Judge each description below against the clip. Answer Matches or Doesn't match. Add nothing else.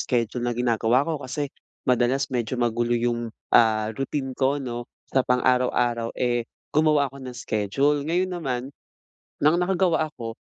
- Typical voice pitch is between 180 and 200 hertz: Doesn't match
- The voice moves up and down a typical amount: Matches